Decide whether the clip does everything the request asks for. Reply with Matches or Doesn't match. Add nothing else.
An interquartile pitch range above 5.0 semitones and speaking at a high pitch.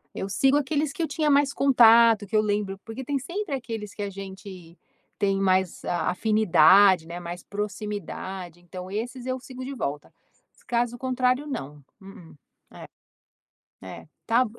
Matches